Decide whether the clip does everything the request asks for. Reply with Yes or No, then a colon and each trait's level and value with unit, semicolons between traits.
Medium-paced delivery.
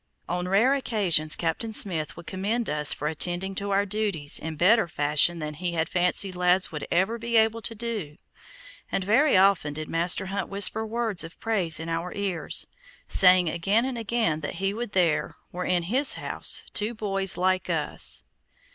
Yes: average, 180 wpm